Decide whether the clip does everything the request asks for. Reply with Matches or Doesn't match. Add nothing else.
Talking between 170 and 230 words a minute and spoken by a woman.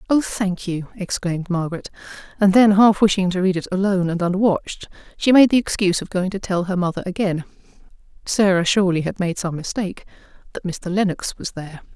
Matches